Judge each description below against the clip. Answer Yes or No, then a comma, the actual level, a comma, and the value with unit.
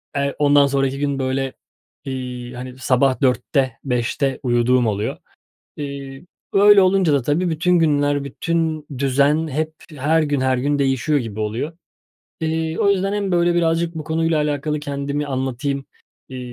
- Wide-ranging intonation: No, average, 3.3 semitones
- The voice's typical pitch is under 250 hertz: Yes, medium, 140 Hz